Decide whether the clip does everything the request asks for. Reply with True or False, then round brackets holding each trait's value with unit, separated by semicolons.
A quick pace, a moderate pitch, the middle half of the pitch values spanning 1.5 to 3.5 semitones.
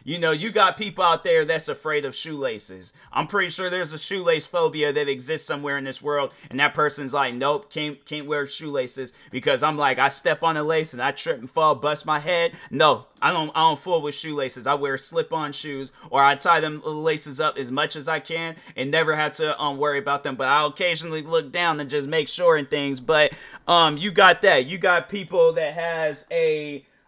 True (225 wpm; 155 Hz; 2.7 semitones)